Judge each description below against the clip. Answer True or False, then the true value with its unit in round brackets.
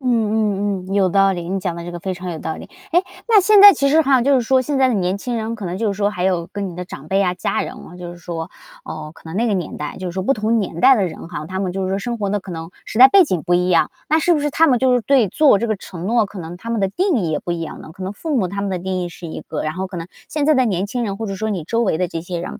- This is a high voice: True (195 Hz)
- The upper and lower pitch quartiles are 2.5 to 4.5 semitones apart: False (4.9 semitones)